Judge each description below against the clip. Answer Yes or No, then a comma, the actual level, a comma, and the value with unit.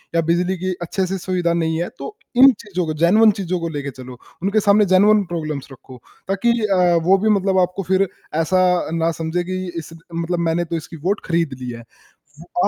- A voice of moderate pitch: Yes, medium, 180 Hz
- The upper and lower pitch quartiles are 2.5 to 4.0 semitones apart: Yes, average, 3.0 semitones